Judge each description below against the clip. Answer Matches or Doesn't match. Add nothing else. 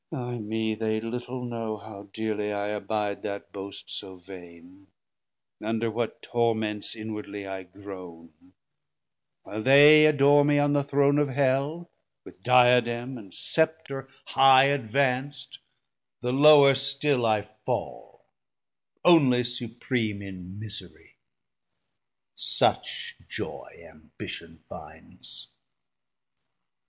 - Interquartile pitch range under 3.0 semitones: Doesn't match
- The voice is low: Matches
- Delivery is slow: Matches